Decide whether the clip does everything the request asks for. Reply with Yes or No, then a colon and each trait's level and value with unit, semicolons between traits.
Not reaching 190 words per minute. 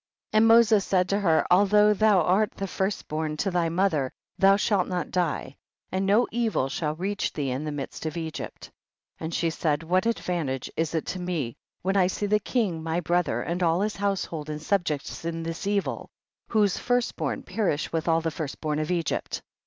No: fast, 205 wpm